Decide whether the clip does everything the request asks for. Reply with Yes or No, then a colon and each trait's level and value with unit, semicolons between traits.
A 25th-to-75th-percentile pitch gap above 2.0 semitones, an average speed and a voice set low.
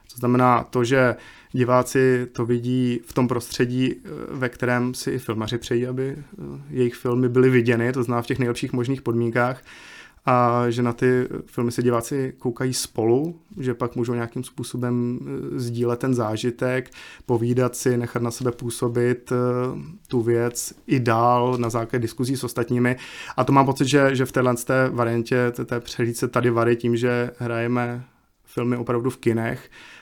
No: narrow, 1.1 semitones; average, 160 wpm; low, 125 Hz